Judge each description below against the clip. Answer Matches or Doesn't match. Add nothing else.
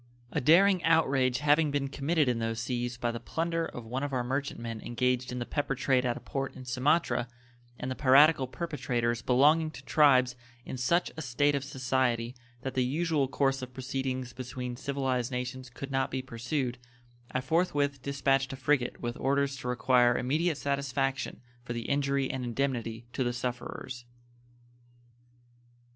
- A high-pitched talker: Doesn't match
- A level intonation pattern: Matches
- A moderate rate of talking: Matches